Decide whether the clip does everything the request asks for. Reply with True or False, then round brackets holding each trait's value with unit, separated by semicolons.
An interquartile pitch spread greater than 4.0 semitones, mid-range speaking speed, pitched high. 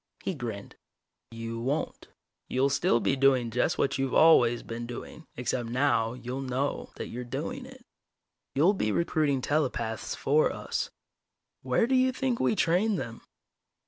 False (5.2 semitones; 150 wpm; 135 Hz)